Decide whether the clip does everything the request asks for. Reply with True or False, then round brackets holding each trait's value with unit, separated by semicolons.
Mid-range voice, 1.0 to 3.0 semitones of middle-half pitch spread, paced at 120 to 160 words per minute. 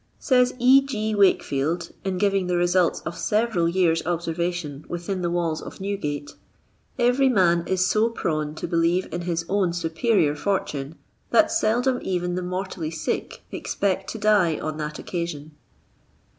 False (180 Hz; 3.5 semitones; 150 wpm)